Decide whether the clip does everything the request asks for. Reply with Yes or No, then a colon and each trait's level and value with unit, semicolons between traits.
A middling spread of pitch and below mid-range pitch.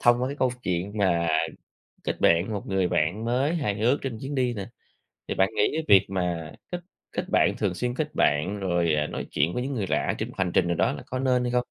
No: wide, 6.0 semitones; low, 105 Hz